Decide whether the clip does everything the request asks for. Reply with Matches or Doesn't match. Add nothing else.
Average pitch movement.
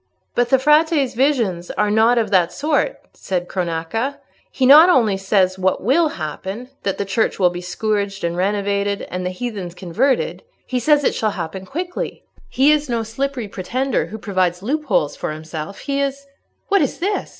Doesn't match